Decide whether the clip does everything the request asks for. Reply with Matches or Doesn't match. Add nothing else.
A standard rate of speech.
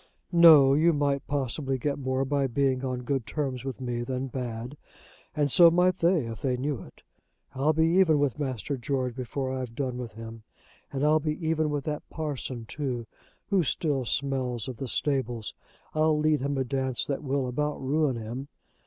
Matches